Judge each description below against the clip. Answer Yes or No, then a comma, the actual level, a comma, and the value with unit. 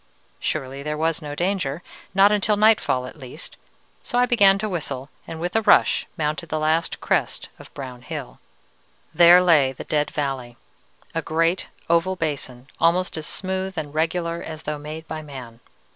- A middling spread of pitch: Yes, average, 3.8 semitones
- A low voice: No, medium, 160 Hz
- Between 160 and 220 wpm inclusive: Yes, average, 170 wpm